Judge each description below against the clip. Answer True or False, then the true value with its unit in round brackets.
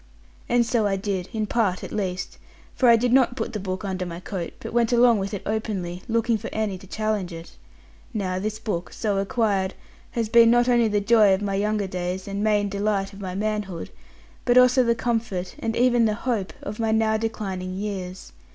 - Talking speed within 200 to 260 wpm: True (205 wpm)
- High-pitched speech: True (210 Hz)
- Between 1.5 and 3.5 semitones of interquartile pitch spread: True (3.1 semitones)